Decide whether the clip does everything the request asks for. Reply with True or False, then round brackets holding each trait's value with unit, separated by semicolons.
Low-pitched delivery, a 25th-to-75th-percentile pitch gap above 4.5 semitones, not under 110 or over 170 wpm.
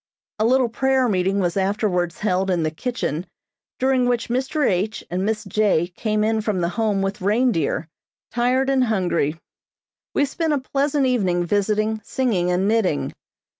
False (215 Hz; 5.4 semitones; 160 wpm)